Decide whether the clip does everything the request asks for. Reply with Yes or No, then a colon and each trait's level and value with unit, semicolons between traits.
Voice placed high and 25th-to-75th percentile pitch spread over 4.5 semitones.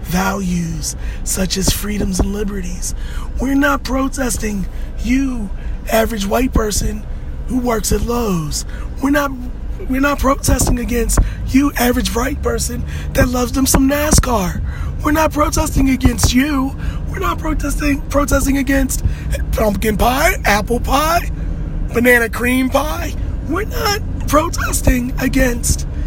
Yes: high, 245 Hz; wide, 5.5 semitones